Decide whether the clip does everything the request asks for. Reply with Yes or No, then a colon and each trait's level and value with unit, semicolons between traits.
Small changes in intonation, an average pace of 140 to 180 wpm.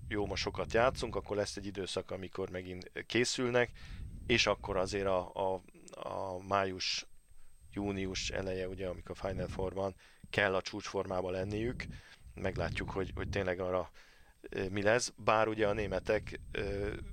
Yes: narrow, 1.9 semitones; average, 145 wpm